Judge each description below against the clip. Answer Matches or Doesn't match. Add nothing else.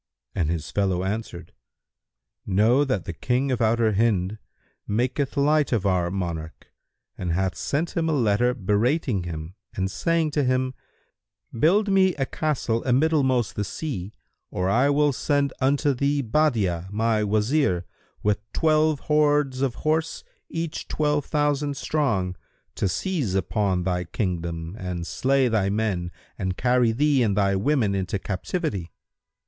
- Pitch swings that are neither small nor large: Doesn't match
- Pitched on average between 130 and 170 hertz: Doesn't match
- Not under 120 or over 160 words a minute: Matches